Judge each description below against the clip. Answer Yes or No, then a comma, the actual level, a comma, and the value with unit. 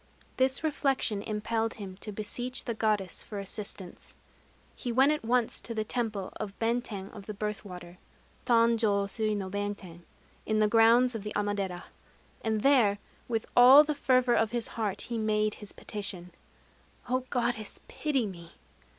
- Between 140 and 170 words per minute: Yes, average, 160 wpm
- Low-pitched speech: No, high, 215 Hz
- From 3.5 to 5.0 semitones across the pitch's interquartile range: No, average, 3.0 semitones